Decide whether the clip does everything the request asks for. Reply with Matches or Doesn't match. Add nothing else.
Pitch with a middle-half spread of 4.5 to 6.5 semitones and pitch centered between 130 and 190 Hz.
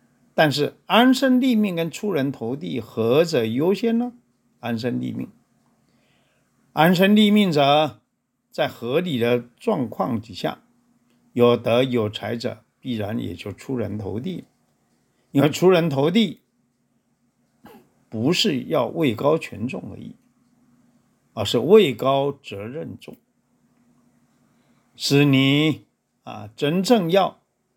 Doesn't match